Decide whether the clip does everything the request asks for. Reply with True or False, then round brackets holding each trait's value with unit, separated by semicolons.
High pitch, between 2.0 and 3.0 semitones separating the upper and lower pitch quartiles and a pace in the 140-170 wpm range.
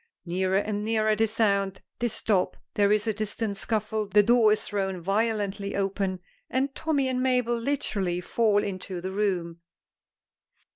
True (210 Hz; 2.5 semitones; 150 wpm)